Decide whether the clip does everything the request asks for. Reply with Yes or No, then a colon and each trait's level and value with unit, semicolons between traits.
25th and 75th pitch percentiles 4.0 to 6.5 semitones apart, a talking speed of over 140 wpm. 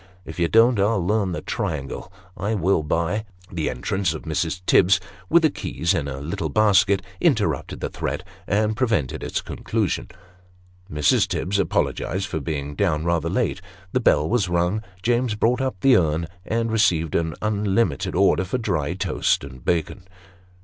Yes: average, 4.9 semitones; average, 165 wpm